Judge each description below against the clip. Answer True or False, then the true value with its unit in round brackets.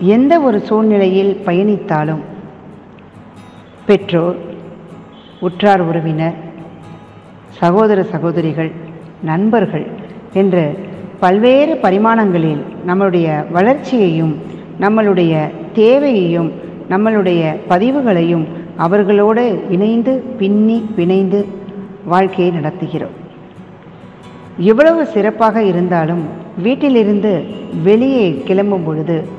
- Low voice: False (190 Hz)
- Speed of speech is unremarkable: False (65 wpm)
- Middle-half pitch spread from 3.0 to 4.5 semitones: True (3.8 semitones)